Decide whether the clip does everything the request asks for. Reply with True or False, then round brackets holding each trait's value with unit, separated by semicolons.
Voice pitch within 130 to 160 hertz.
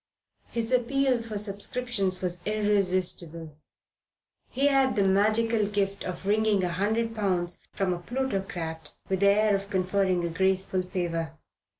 False (200 Hz)